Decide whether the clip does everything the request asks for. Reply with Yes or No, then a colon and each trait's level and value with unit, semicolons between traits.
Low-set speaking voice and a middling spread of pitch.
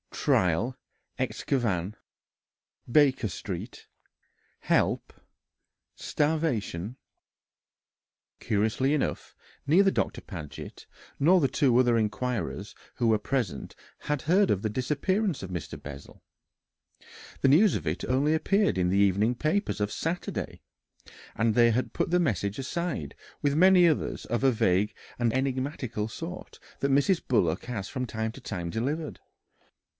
No: low, 125 Hz; wide, 6.2 semitones